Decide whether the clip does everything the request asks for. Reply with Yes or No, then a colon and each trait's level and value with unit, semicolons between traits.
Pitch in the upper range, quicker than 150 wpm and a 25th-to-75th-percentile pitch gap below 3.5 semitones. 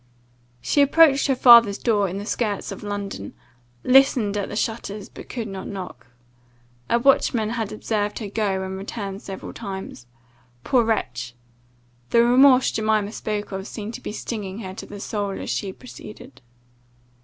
Yes: high, 210 Hz; average, 160 wpm; average, 3.0 semitones